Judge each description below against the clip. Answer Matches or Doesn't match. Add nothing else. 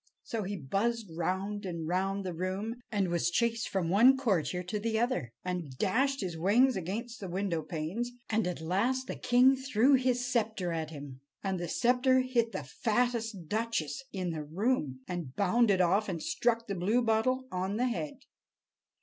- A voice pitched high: Matches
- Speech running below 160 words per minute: Doesn't match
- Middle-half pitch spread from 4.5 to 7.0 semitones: Matches